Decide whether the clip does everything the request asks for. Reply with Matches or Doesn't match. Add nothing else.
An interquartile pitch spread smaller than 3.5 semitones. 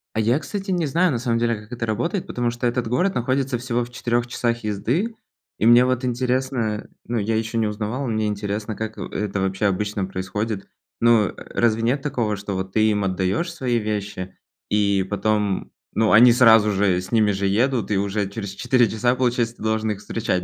Matches